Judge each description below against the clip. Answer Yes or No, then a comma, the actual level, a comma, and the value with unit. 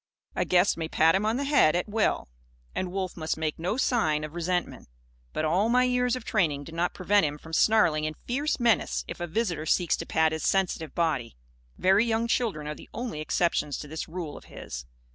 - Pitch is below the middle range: No, medium, 175 Hz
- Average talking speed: No, fast, 215 wpm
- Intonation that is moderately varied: No, wide, 6.0 semitones